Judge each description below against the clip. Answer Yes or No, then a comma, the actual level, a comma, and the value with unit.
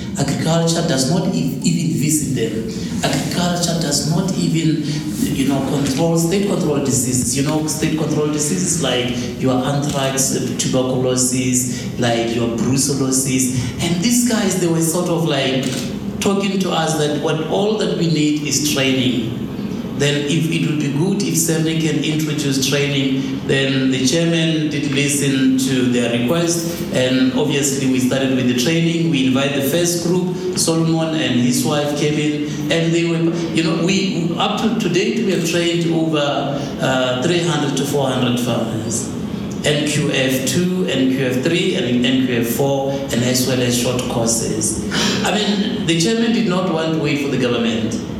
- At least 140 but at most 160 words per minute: Yes, average, 155 wpm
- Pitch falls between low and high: Yes, medium, 150 Hz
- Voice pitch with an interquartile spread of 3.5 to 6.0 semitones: Yes, average, 4.3 semitones